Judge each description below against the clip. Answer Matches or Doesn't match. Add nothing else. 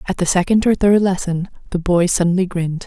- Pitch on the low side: Doesn't match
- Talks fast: Matches